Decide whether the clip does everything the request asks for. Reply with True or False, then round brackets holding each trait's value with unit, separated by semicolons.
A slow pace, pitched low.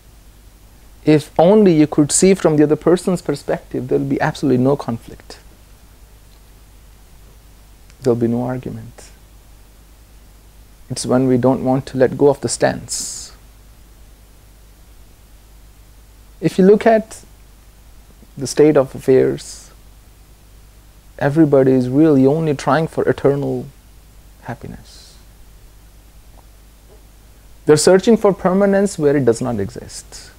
True (115 wpm; 115 Hz)